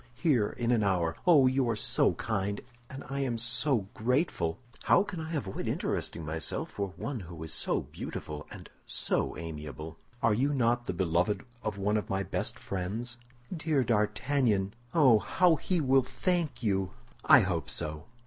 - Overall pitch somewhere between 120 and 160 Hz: No, low, 110 Hz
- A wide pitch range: Yes, wide, 6.1 semitones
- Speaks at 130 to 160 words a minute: No, average, 170 wpm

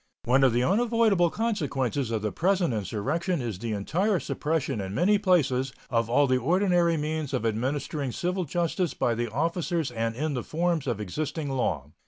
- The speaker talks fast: No, average, 175 wpm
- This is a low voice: No, medium, 145 Hz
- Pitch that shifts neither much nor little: No, wide, 6.5 semitones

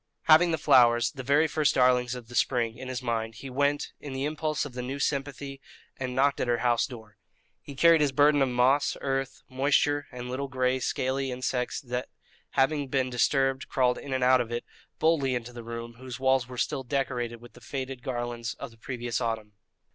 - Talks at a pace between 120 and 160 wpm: No, fast, 205 wpm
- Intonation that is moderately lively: No, narrow, 2.3 semitones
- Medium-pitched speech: No, low, 130 Hz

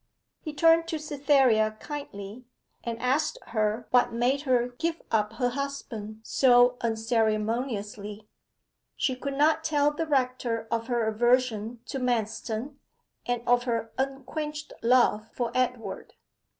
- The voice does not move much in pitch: No, average, 3.7 semitones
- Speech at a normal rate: No, slow, 125 wpm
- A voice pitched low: No, high, 245 Hz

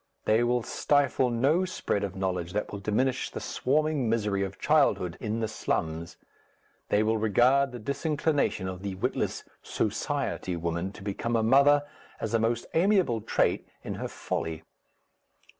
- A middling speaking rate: Yes, average, 155 wpm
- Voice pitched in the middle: No, low, 110 Hz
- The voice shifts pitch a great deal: Yes, wide, 5.7 semitones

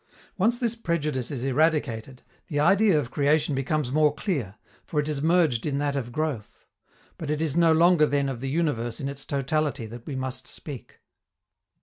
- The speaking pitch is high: No, medium, 145 Hz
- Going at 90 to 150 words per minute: No, average, 185 wpm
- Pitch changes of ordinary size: Yes, average, 3.2 semitones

